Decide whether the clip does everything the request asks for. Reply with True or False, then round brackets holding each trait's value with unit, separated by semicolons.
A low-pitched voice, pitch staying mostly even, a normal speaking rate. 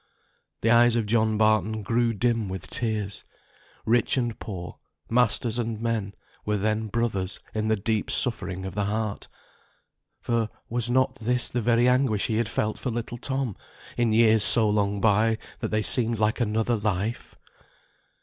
True (110 Hz; 1.9 semitones; 165 wpm)